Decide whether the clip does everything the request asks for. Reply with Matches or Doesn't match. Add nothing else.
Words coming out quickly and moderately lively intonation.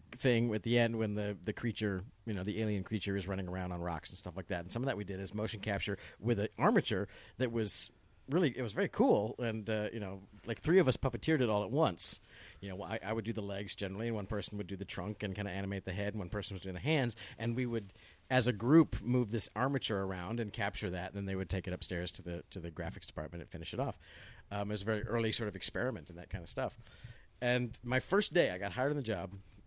Matches